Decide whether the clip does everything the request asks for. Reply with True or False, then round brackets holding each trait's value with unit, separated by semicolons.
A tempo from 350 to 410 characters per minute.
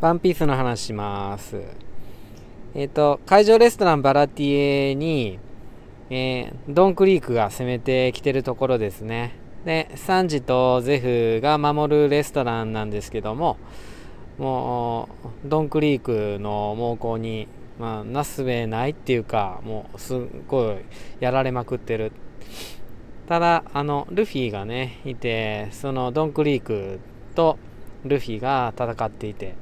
False (265 characters per minute)